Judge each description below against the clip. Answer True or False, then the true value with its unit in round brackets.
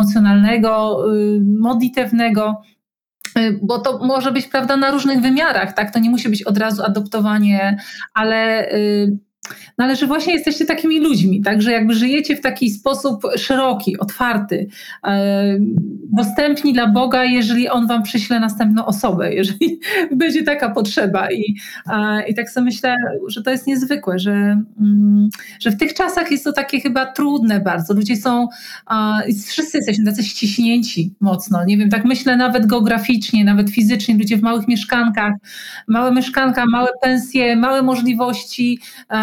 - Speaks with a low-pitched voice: False (230 Hz)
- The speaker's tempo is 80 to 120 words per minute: False (155 wpm)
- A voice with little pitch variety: False (3.7 semitones)